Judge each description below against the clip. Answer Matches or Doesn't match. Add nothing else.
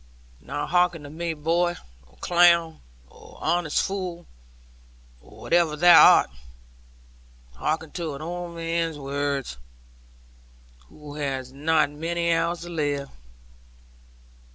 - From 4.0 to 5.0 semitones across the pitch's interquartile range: Doesn't match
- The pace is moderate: Doesn't match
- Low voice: Doesn't match